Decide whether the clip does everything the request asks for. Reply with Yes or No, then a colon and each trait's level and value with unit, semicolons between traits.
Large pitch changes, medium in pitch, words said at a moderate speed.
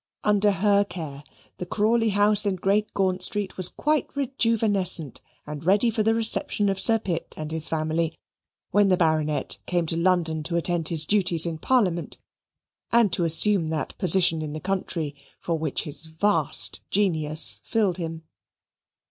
No: average, 4.4 semitones; medium, 180 Hz; average, 160 wpm